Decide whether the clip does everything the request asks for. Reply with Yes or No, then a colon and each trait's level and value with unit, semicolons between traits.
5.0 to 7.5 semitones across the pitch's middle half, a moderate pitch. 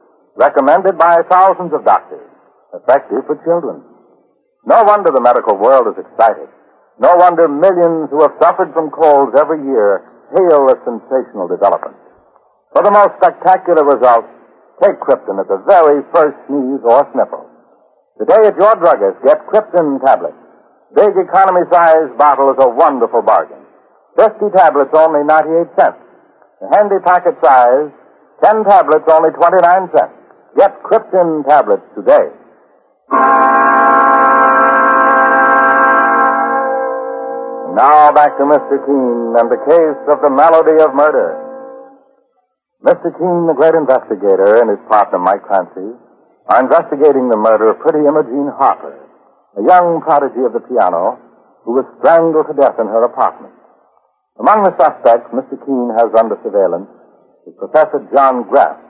Yes: wide, 5.4 semitones; medium, 160 Hz